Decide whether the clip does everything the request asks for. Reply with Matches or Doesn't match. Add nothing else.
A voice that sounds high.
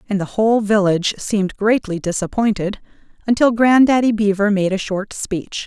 Matches